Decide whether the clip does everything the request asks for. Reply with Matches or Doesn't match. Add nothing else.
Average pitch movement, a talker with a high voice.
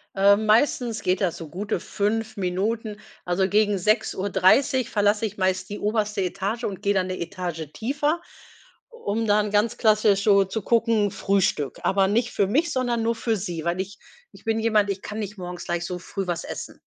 Matches